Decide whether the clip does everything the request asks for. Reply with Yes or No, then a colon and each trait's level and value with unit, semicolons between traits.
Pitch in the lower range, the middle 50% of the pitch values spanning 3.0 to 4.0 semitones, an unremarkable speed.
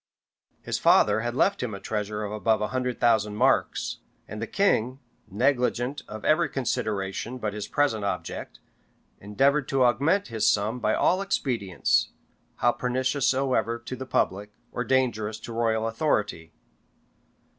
Yes: low, 115 Hz; average, 3.5 semitones; average, 145 wpm